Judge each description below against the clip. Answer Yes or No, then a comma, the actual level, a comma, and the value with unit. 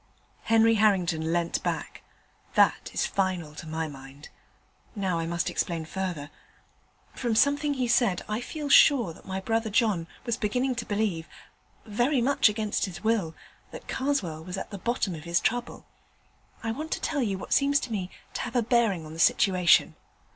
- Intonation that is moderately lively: No, wide, 5.8 semitones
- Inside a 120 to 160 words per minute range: No, average, 175 wpm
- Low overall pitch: No, high, 205 Hz